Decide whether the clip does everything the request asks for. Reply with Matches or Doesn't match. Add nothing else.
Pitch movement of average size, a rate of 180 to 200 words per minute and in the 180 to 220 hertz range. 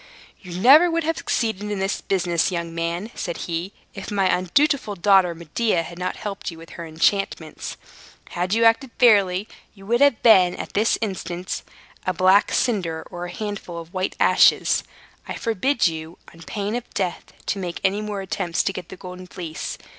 Matches